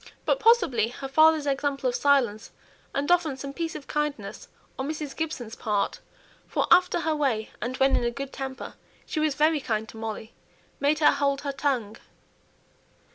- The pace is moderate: Yes, average, 175 wpm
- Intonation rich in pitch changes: No, average, 3.7 semitones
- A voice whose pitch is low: No, very high, 275 Hz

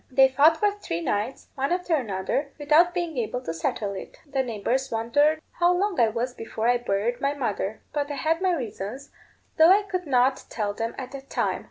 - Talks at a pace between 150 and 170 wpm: No, fast, 205 wpm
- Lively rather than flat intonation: Yes, wide, 5.7 semitones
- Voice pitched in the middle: No, very high, 265 Hz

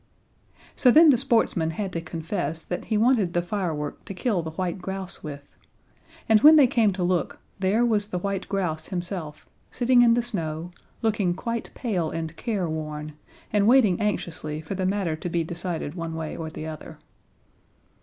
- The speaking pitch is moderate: Yes, medium, 180 Hz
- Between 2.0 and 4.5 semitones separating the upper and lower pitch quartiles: No, average, 4.9 semitones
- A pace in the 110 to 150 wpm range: No, average, 175 wpm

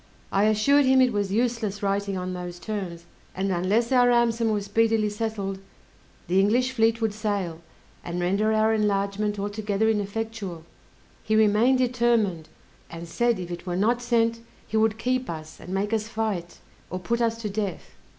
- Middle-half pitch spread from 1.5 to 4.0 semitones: Yes, average, 2.8 semitones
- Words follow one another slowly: No, average, 170 wpm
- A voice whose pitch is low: No, high, 210 Hz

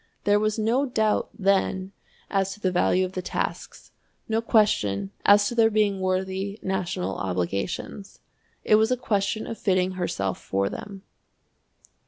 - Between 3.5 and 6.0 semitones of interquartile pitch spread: No, average, 2.7 semitones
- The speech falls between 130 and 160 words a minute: Yes, average, 150 wpm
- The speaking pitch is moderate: No, high, 195 Hz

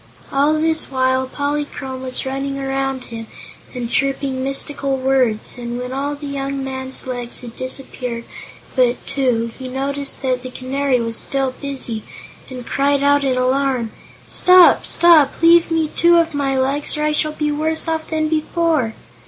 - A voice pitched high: Yes, very high, 270 Hz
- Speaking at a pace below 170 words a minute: Yes, average, 160 wpm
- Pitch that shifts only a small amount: Yes, narrow, 2.2 semitones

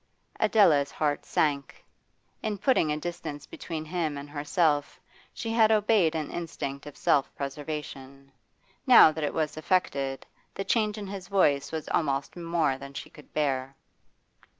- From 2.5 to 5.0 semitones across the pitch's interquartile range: Yes, average, 4.0 semitones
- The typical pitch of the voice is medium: Yes, medium, 155 Hz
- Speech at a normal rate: Yes, average, 150 wpm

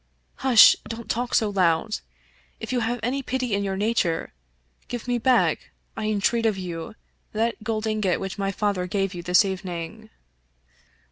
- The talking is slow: No, average, 175 wpm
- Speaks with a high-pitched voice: Yes, high, 215 Hz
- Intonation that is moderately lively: Yes, average, 3.6 semitones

